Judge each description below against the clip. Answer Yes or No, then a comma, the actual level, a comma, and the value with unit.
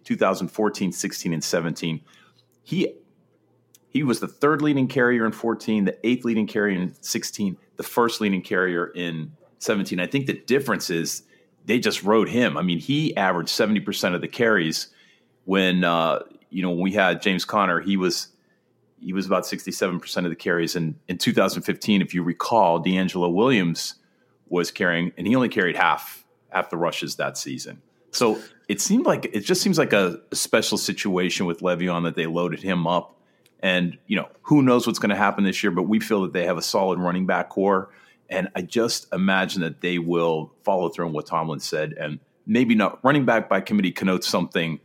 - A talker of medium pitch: No, very low, 95 Hz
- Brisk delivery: No, average, 190 wpm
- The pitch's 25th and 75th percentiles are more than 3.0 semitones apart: Yes, average, 3.9 semitones